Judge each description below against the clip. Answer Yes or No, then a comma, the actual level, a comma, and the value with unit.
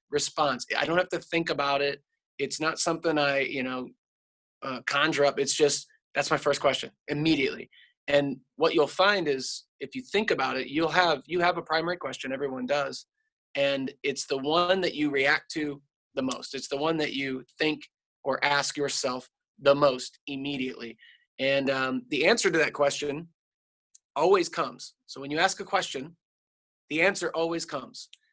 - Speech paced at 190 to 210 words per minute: No, average, 180 wpm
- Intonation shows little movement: No, average, 3.8 semitones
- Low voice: No, medium, 145 Hz